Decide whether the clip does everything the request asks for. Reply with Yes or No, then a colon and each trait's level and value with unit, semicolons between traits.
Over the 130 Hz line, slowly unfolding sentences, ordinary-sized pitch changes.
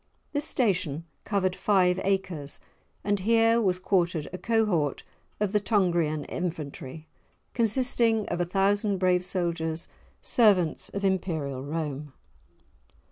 Yes: medium, 185 Hz; slow, 115 wpm; average, 4.1 semitones